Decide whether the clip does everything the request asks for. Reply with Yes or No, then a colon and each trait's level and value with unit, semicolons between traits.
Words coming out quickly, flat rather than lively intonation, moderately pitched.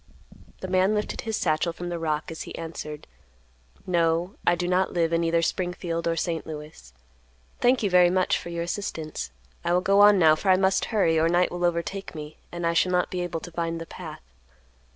Yes: fast, 215 wpm; narrow, 1.9 semitones; medium, 170 Hz